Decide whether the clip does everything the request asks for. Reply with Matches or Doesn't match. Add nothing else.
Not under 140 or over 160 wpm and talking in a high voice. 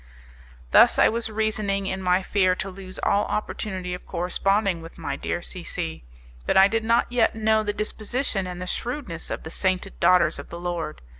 Doesn't match